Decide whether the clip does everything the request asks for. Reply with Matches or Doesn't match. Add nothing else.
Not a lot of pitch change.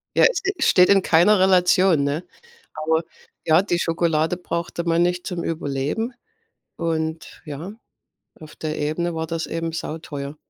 Matches